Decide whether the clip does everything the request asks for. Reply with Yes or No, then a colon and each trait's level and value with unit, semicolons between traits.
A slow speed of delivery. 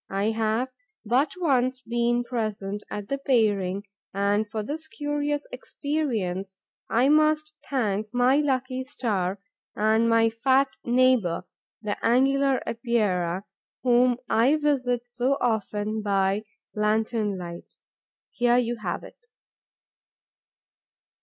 Yes: slow, 110 wpm